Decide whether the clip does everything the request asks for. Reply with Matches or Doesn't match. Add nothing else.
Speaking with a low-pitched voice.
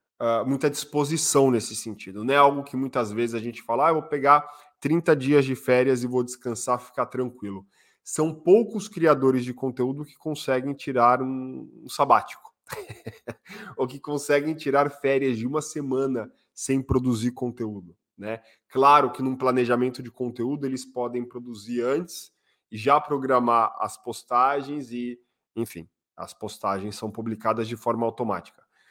Matches